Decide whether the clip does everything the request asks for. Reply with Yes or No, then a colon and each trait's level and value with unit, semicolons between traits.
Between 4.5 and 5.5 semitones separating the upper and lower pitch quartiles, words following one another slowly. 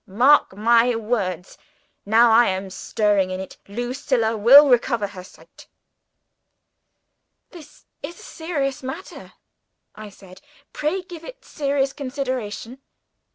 Yes: average, 5.2 semitones; slow, 115 wpm